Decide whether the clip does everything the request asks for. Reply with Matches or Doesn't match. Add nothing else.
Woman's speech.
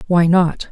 Matches